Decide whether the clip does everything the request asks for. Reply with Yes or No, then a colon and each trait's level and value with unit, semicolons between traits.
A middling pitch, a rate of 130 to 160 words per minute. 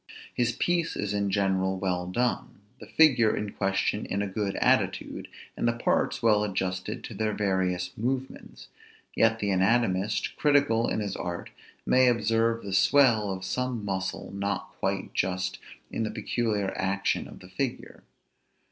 No: low, 105 Hz; average, 155 wpm